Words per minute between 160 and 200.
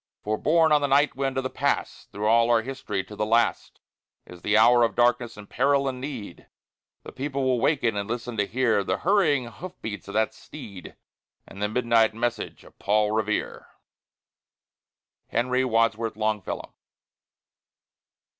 Yes: average, 165 wpm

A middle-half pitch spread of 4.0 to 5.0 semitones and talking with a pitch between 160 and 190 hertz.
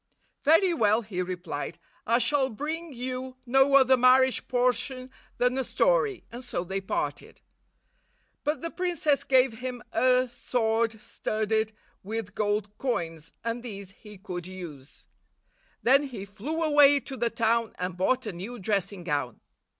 No: average, 4.6 semitones; high, 235 Hz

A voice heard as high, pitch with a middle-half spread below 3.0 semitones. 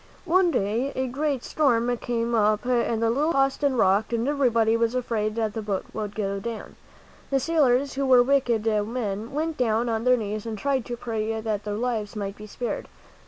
No: high, 230 Hz; average, 3.3 semitones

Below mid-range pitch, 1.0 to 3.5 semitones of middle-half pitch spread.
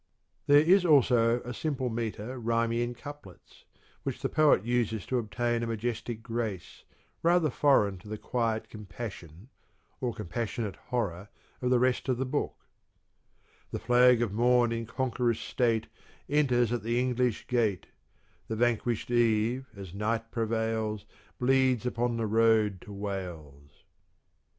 Yes: low, 115 Hz; narrow, 2.5 semitones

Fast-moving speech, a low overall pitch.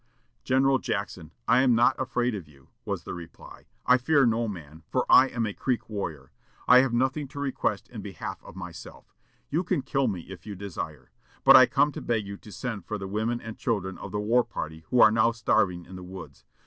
Yes: fast, 220 wpm; low, 110 Hz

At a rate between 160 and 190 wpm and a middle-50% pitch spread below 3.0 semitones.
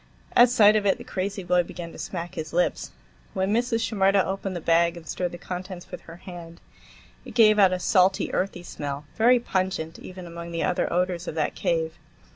No: fast, 205 wpm; narrow, 2.5 semitones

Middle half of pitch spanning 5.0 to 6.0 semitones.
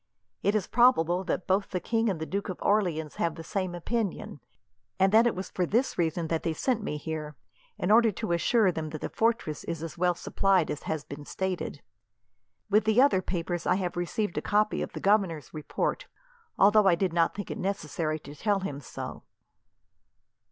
No: average, 4.2 semitones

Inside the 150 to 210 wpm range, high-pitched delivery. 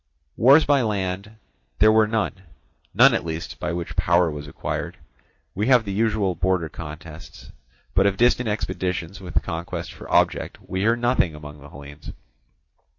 No: average, 155 wpm; very low, 95 Hz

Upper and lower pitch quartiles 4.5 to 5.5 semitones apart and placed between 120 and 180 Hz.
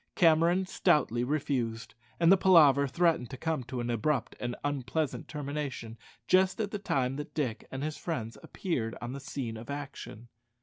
Yes: average, 4.9 semitones; medium, 140 Hz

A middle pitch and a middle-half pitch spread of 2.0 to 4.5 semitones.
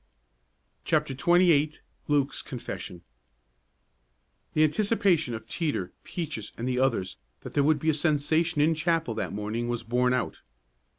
No: medium, 145 Hz; average, 4.9 semitones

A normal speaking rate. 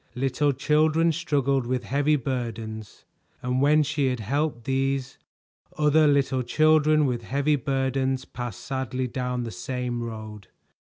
No: slow, 130 wpm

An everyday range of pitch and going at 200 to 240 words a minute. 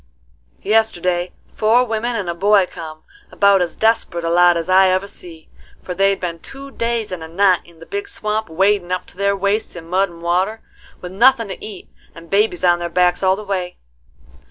Yes: average, 3.4 semitones; fast, 205 wpm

